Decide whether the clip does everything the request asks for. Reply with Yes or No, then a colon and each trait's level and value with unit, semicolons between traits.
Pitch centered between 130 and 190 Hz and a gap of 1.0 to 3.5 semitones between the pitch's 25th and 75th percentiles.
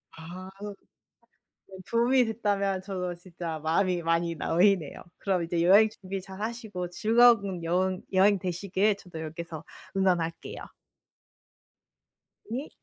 Yes: medium, 185 Hz; average, 2.9 semitones